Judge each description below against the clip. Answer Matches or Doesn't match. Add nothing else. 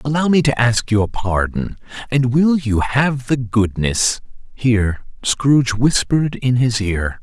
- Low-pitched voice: Matches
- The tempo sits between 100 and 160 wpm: Matches